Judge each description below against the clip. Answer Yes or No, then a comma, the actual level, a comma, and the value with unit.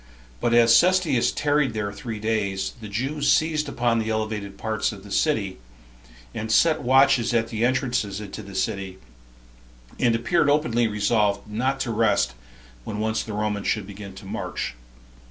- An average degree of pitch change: Yes, average, 3.7 semitones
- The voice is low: Yes, low, 110 Hz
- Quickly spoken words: No, average, 160 wpm